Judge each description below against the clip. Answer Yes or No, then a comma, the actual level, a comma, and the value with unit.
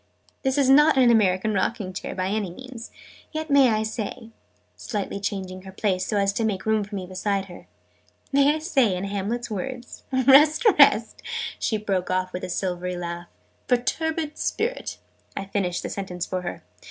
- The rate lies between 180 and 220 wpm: Yes, average, 185 wpm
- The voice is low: No, high, 210 Hz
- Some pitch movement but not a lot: No, wide, 5.8 semitones